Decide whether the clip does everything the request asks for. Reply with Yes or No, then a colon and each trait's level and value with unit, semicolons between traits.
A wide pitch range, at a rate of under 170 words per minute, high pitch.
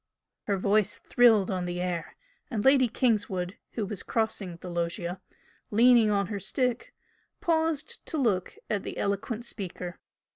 No: average, 4.5 semitones; average, 145 wpm; high, 205 Hz